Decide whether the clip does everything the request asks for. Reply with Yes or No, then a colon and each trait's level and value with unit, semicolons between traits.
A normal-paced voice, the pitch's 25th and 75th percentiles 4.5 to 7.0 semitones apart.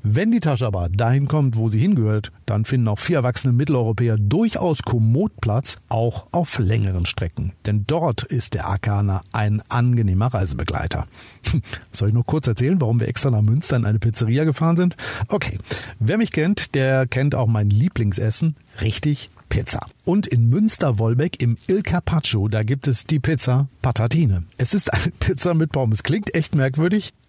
Yes: average, 170 wpm; average, 5.0 semitones